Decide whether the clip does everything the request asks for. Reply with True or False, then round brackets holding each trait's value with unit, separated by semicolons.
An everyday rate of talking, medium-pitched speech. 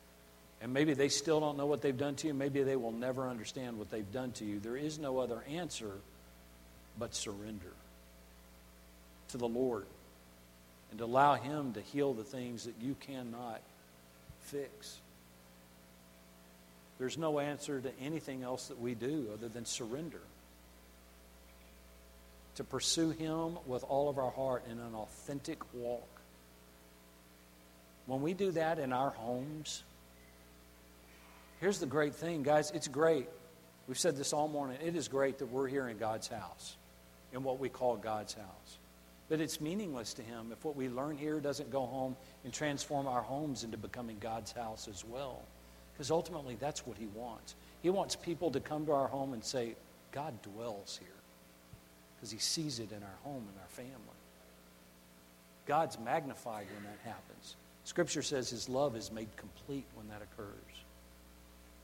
False (160 wpm; 115 Hz)